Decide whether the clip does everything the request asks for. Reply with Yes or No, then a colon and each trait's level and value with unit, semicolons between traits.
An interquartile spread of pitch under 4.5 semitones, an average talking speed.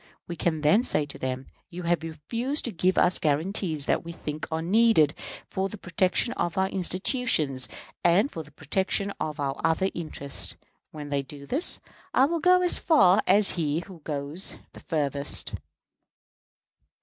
No: average, 4.8 semitones; average, 165 wpm